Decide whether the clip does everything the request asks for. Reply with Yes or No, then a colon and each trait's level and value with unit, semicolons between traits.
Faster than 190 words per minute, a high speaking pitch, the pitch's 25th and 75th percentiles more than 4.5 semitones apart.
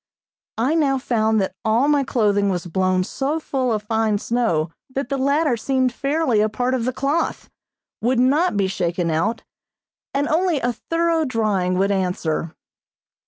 No: average, 165 wpm; high, 235 Hz; wide, 5.6 semitones